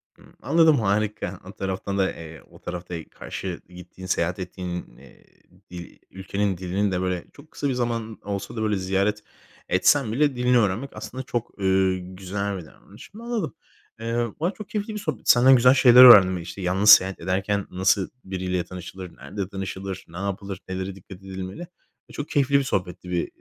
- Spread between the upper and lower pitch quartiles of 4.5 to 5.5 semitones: No, average, 4.1 semitones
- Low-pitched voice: Yes, very low, 95 Hz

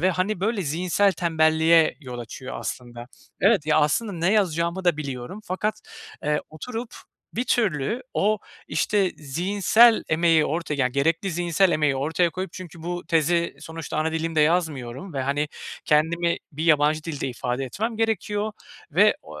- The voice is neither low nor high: Yes, medium, 165 Hz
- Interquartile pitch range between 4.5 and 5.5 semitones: No, average, 4.0 semitones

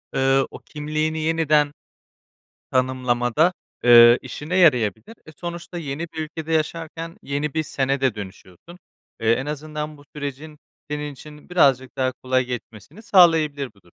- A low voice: No, medium, 150 Hz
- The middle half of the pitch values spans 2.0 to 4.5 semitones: Yes, average, 3.6 semitones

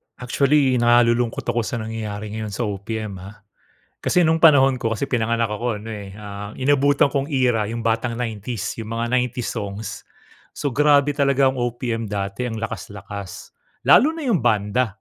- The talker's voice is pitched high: No, low, 115 Hz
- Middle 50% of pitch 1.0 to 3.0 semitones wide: No, average, 3.6 semitones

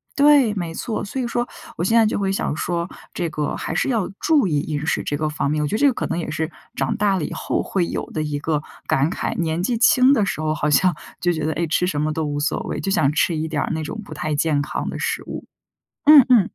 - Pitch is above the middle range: No, medium, 170 Hz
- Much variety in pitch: Yes, wide, 5.8 semitones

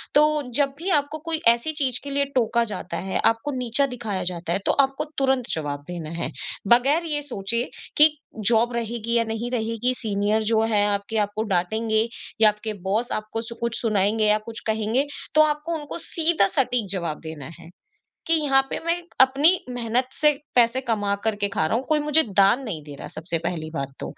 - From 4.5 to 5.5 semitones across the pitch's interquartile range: Yes, average, 4.8 semitones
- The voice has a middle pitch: No, high, 230 Hz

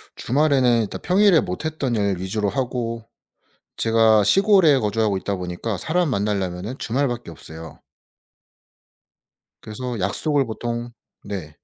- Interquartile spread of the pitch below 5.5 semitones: Yes, average, 5.1 semitones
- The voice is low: Yes, low, 115 Hz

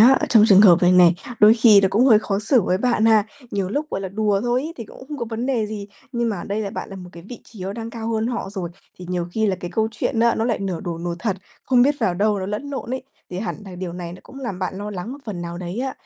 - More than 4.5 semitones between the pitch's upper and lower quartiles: No, average, 3.9 semitones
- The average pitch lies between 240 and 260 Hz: No, high, 210 Hz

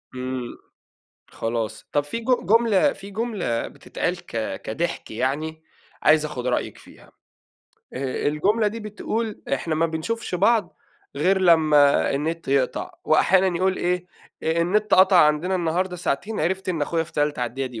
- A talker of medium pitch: Yes, medium, 165 Hz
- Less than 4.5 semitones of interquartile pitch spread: No, average, 4.8 semitones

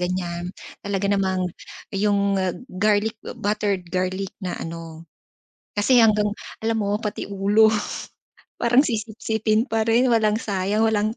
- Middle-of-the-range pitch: No, high, 205 Hz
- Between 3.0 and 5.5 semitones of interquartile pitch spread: No, narrow, 2.6 semitones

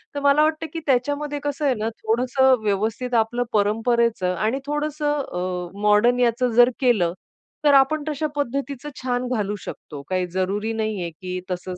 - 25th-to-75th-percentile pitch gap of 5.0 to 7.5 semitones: Yes, average, 5.3 semitones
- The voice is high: Yes, high, 240 Hz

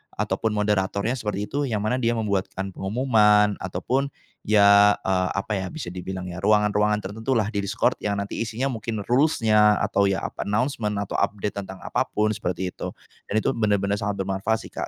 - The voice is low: Yes, low, 105 Hz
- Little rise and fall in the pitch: Yes, narrow, 2.1 semitones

